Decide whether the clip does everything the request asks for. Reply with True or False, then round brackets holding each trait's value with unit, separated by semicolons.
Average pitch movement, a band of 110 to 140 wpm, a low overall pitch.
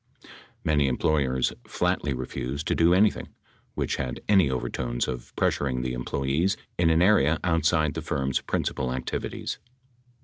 True (4.3 semitones; 135 wpm; 70 Hz)